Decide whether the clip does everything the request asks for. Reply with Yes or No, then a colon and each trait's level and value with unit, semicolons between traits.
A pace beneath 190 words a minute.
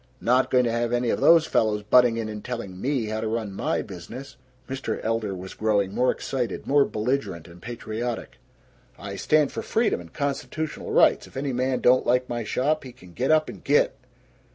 No: average, 200 wpm